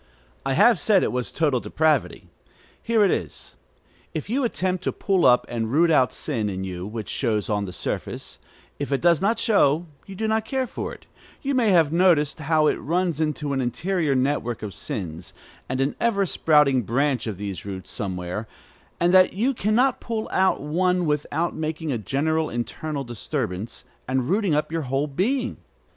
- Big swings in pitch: Yes, wide, 7.1 semitones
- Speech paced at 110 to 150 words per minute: No, average, 185 wpm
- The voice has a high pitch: No, medium, 150 Hz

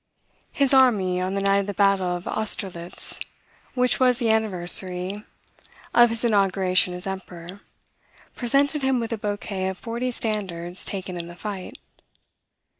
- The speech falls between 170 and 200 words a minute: No, average, 145 wpm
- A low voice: No, high, 200 Hz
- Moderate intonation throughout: Yes, average, 3.9 semitones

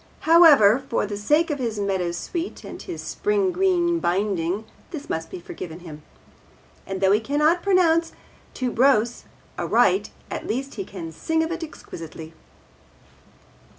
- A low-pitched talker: No, high, 245 Hz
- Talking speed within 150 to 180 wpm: No, average, 140 wpm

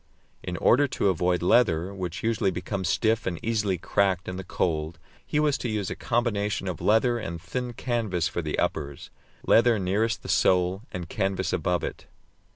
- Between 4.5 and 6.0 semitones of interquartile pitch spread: No, average, 4.1 semitones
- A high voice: No, very low, 95 Hz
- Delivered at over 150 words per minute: Yes, average, 175 wpm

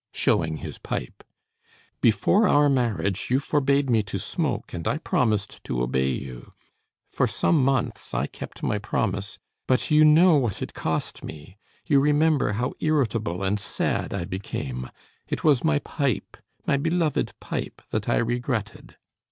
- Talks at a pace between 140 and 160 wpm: Yes, average, 150 wpm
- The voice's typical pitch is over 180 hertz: No, low, 120 Hz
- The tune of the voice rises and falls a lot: Yes, wide, 7.0 semitones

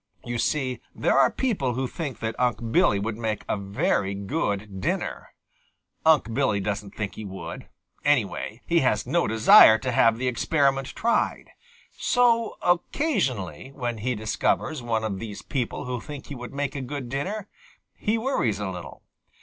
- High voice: No, low, 120 Hz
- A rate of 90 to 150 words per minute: No, average, 165 wpm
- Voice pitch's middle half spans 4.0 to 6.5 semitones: Yes, average, 5.0 semitones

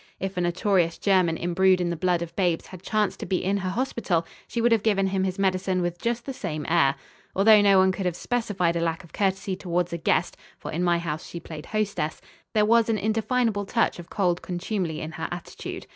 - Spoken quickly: Yes, fast, 225 wpm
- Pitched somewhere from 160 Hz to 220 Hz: Yes, medium, 185 Hz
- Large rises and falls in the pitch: No, average, 3.1 semitones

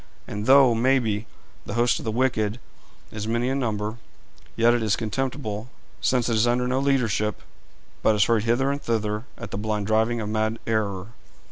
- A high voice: No, low, 115 Hz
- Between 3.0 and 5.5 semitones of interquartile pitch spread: No, narrow, 2.5 semitones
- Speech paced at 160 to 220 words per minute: Yes, average, 180 wpm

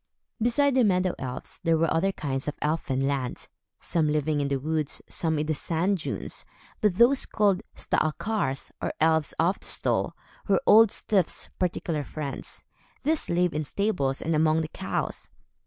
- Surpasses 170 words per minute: No, average, 165 wpm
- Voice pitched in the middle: Yes, medium, 160 Hz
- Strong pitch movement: No, average, 4.6 semitones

